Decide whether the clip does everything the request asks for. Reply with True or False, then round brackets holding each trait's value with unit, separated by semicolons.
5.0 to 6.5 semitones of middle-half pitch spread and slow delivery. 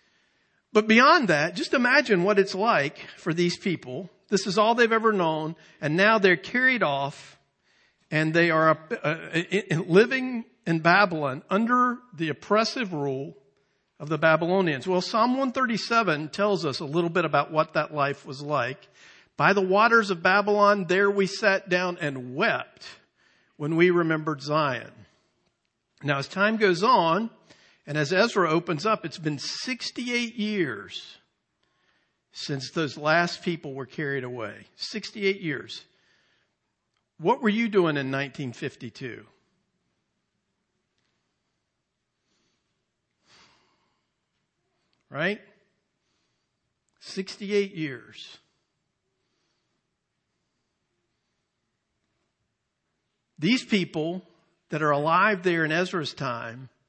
True (5.3 semitones; 110 wpm)